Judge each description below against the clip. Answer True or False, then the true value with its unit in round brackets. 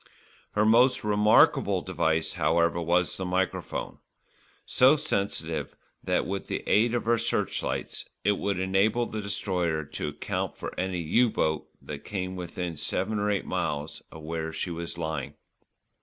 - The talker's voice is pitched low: True (90 Hz)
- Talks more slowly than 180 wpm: True (150 wpm)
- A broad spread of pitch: False (4.1 semitones)